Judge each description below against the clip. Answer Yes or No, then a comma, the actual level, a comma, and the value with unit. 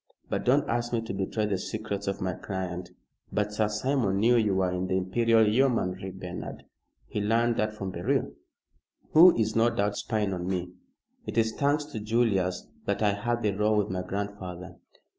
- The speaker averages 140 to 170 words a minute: No, average, 185 wpm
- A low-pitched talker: Yes, low, 105 Hz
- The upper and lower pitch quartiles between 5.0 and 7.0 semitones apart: No, average, 3.4 semitones